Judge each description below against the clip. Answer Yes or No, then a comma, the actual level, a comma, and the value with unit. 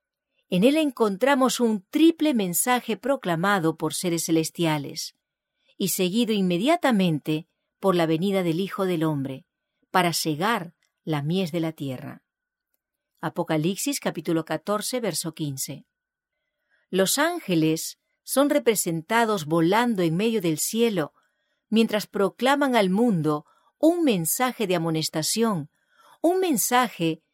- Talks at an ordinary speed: No, slow, 110 wpm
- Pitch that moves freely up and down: Yes, wide, 7.5 semitones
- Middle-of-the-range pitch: No, high, 195 Hz